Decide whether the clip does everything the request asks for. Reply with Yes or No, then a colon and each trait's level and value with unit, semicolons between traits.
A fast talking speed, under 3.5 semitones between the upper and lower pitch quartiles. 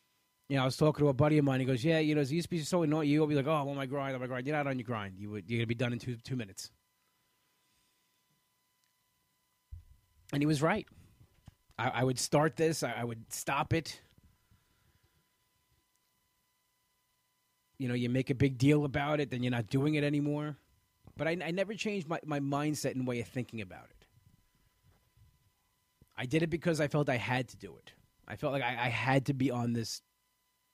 No: fast, 215 wpm; average, 4.1 semitones